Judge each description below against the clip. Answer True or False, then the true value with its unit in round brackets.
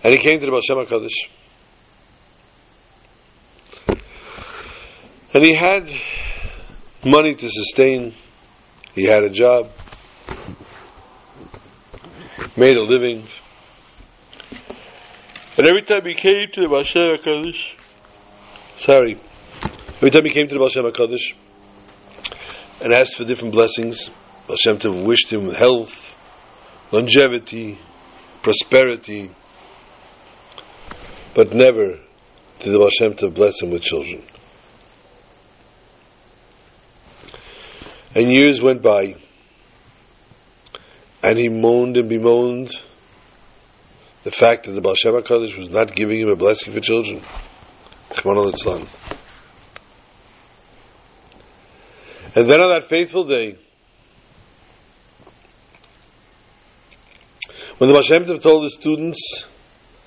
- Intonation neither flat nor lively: False (6.1 semitones)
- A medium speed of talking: False (95 wpm)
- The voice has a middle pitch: False (120 Hz)